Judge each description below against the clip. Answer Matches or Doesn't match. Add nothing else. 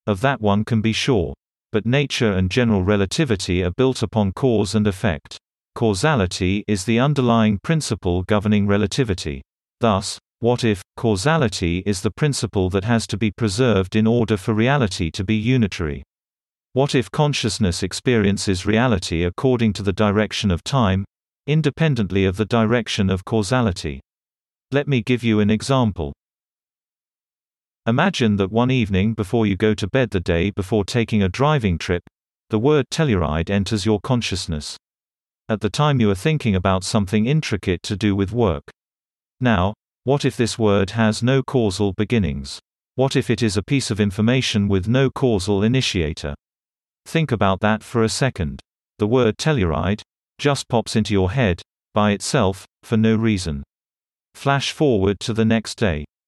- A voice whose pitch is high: Doesn't match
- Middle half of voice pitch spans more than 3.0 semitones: Matches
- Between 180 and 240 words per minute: Doesn't match